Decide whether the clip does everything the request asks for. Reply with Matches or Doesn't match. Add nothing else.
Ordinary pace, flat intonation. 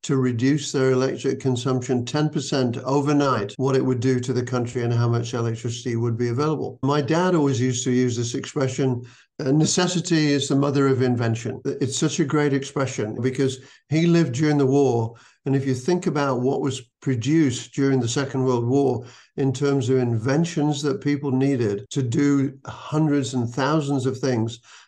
Matches